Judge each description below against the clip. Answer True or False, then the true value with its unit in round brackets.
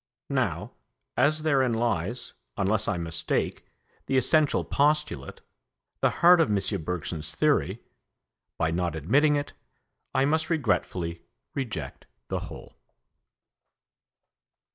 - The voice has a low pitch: True (115 Hz)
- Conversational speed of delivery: False (105 wpm)